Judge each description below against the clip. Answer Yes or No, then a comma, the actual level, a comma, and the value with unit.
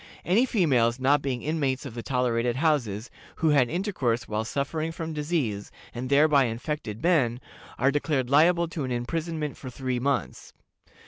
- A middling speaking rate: Yes, average, 155 wpm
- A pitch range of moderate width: Yes, average, 4.5 semitones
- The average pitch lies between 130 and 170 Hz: Yes, medium, 140 Hz